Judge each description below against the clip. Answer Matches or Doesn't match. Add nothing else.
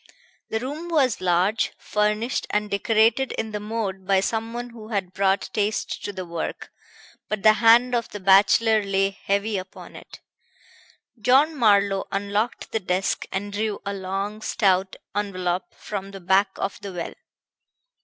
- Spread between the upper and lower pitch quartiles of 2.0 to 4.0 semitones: Matches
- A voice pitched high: Matches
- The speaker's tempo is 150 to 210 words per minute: Matches